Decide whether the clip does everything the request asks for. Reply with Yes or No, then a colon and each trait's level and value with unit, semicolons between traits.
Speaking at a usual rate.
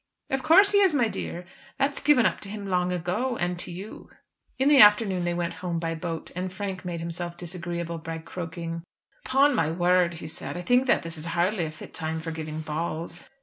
No: fast, 215 wpm